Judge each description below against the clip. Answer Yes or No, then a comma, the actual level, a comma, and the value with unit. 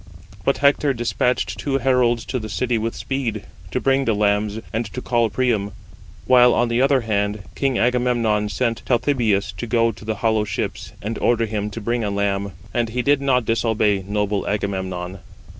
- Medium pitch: No, low, 115 Hz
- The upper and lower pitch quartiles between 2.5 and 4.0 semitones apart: Yes, average, 3.2 semitones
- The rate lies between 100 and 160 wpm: No, average, 180 wpm